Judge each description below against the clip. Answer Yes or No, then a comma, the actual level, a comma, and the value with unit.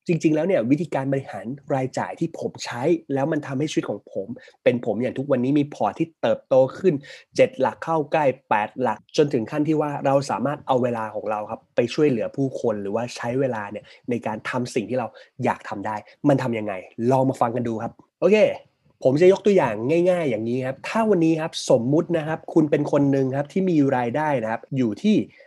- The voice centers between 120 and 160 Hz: Yes, medium, 140 Hz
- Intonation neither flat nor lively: Yes, average, 4.6 semitones